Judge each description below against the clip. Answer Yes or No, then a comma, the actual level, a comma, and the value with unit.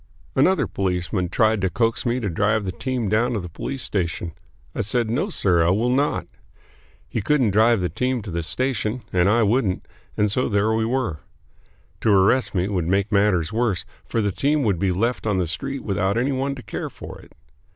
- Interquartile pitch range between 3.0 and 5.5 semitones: Yes, average, 4.5 semitones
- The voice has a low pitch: Yes, low, 105 Hz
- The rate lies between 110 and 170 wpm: No, fast, 205 wpm